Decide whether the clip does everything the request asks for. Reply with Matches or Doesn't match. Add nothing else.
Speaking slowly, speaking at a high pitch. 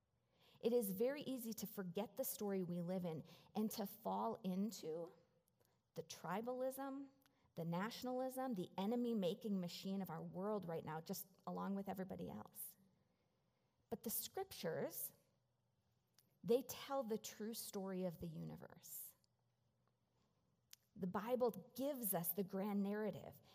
Matches